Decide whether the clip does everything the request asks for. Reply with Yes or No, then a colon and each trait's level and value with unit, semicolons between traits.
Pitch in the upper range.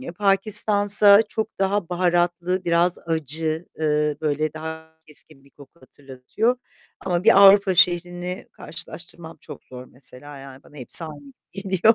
No: medium, 170 Hz